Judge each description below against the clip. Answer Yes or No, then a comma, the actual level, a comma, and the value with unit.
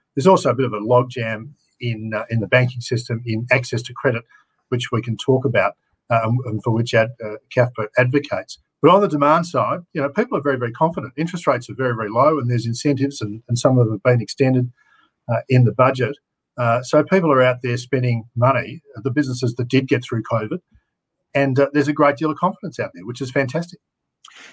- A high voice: No, low, 125 Hz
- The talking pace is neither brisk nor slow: No, fast, 225 wpm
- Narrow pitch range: No, average, 3.3 semitones